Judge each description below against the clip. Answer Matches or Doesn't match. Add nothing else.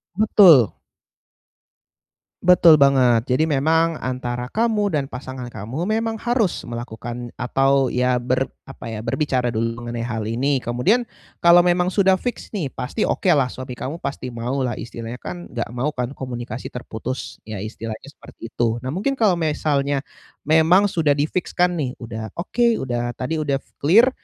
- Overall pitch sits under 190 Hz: Matches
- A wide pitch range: Matches